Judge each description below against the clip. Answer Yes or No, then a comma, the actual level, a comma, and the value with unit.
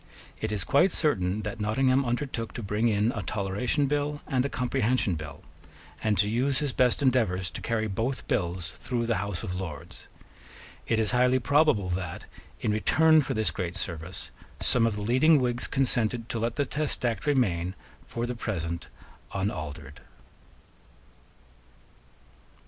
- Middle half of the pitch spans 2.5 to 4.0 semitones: No, average, 5.1 semitones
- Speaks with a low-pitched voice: Yes, low, 115 Hz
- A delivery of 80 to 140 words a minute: No, average, 155 wpm